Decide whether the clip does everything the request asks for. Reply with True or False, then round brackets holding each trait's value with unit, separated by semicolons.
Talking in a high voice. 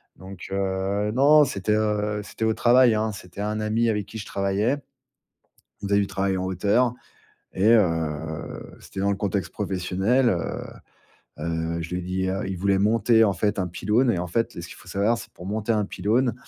False (100 Hz)